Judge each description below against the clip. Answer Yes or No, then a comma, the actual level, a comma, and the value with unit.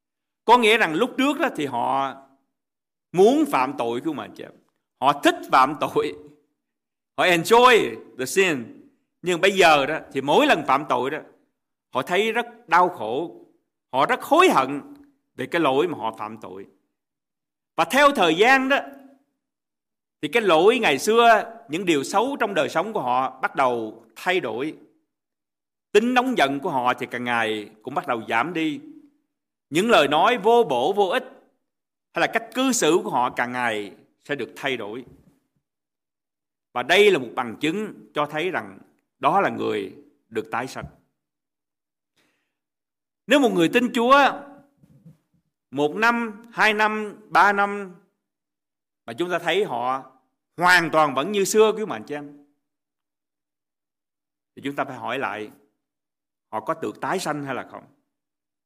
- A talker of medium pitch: No, high, 200 Hz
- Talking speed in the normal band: No, slow, 160 wpm